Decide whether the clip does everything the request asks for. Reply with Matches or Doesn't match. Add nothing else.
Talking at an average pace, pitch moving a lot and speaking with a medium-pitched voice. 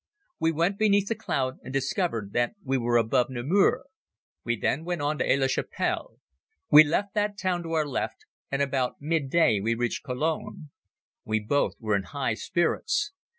Matches